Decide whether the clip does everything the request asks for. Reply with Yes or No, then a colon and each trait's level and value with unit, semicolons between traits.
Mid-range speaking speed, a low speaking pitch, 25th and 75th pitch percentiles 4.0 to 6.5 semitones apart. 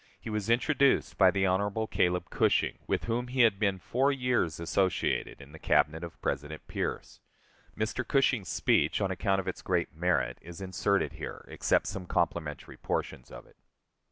Yes: average, 170 wpm; very low, 95 Hz; average, 4.7 semitones